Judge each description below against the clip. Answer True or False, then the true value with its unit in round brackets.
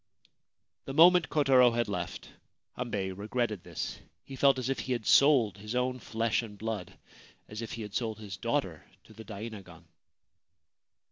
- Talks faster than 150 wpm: True (175 wpm)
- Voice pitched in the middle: False (115 Hz)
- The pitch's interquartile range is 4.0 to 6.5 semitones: False (3.5 semitones)